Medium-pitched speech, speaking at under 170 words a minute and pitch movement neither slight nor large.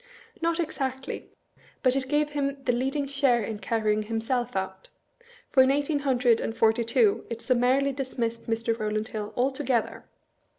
No: very high, 250 Hz; average, 160 wpm; average, 3.3 semitones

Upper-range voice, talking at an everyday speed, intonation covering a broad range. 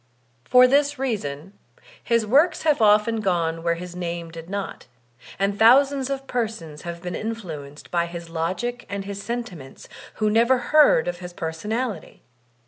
Yes: high, 200 Hz; average, 155 wpm; wide, 6.1 semitones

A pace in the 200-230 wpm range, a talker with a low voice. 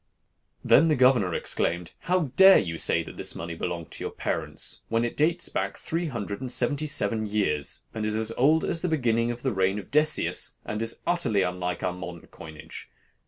Yes: fast, 205 wpm; low, 115 Hz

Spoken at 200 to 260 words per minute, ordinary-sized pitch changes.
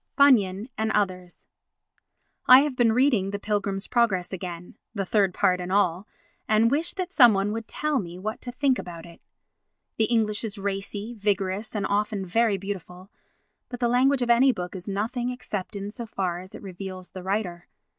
No: average, 175 wpm; average, 4.0 semitones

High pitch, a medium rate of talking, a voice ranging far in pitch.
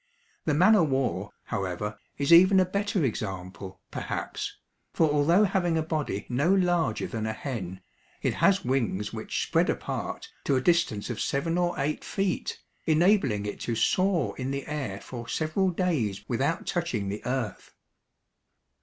No: medium, 140 Hz; average, 155 wpm; wide, 8.2 semitones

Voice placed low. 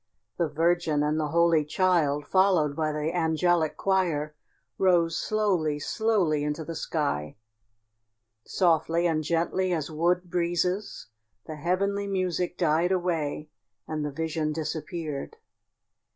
No: medium, 165 Hz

